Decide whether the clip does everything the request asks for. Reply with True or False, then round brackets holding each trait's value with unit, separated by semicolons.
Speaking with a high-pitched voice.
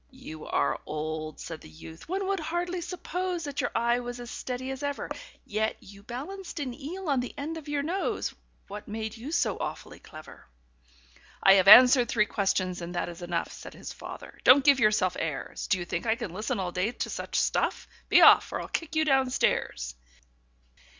True (245 Hz)